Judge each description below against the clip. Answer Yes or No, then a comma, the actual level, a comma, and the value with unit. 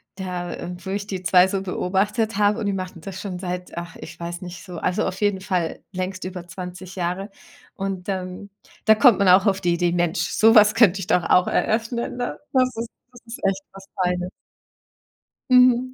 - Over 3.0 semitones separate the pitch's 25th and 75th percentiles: No, narrow, 2.5 semitones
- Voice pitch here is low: No, high, 190 Hz